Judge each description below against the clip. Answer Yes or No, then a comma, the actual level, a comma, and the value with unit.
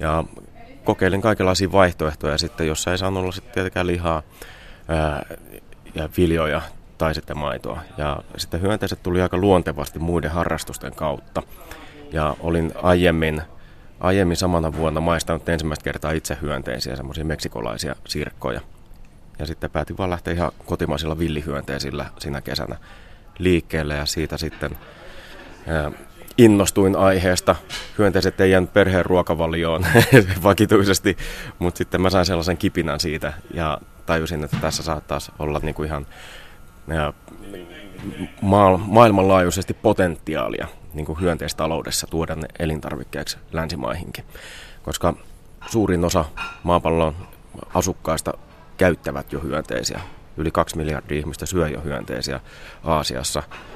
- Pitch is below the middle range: Yes, very low, 80 Hz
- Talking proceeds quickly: No, average, 115 wpm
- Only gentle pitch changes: No, average, 3.2 semitones